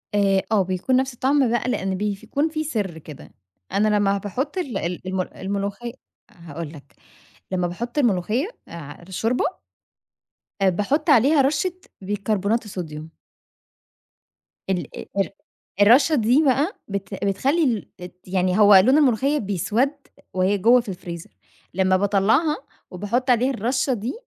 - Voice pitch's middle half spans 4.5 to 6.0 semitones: Yes, wide, 5.5 semitones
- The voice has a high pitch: Yes, high, 205 Hz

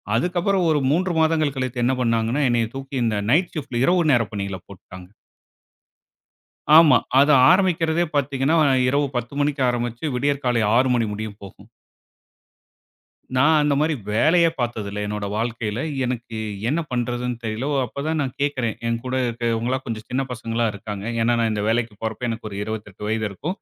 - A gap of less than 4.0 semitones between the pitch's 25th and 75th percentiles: No, average, 4.3 semitones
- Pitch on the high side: No, low, 120 Hz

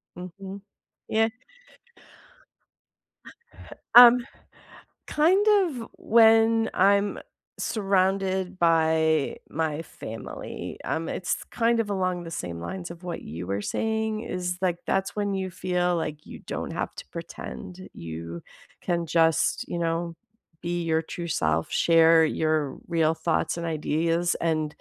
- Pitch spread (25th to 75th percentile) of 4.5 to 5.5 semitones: No, average, 3.6 semitones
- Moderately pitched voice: Yes, medium, 175 Hz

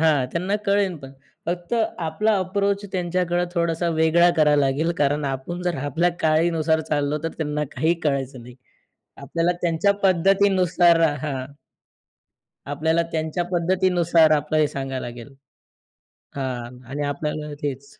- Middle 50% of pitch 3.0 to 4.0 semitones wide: Yes, average, 3.5 semitones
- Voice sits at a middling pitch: Yes, medium, 160 Hz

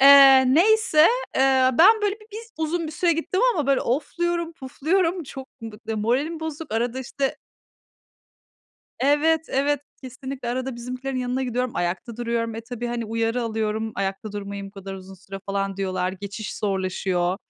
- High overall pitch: Yes, very high, 250 Hz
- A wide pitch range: Yes, wide, 5.9 semitones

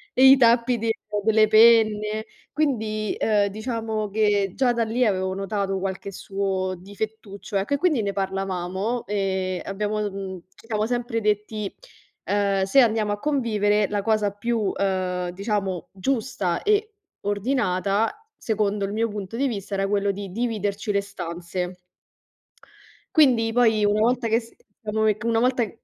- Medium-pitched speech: No, high, 210 Hz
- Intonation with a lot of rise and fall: No, narrow, 2.6 semitones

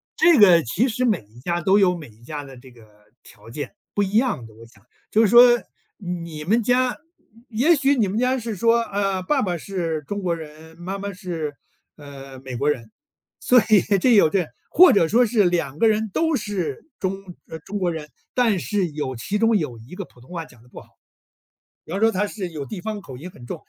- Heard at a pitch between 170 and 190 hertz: Yes, medium, 185 Hz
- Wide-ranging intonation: Yes, wide, 6.5 semitones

